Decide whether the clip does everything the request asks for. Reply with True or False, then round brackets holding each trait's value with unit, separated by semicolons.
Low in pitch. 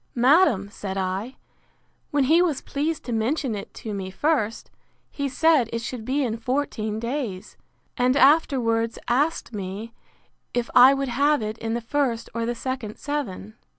False (240 Hz)